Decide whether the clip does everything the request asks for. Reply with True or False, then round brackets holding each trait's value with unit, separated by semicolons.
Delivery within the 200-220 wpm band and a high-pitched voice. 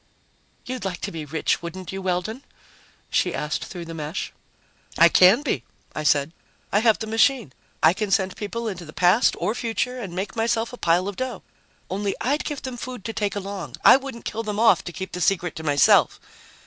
True (205 wpm; 195 Hz)